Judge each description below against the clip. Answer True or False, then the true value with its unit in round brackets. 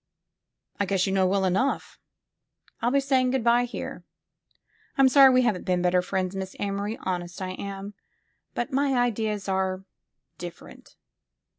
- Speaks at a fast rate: False (150 wpm)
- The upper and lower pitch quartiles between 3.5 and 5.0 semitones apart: True (4.6 semitones)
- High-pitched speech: True (200 Hz)